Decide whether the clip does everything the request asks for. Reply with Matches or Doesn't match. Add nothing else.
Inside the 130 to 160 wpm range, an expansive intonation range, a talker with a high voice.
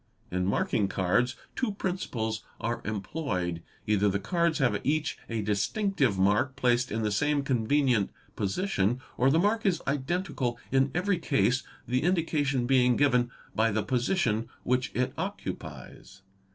Doesn't match